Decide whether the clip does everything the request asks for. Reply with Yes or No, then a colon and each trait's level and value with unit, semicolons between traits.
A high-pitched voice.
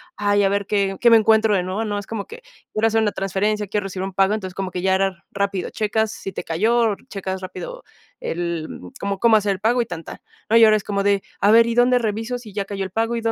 Yes: high, 205 Hz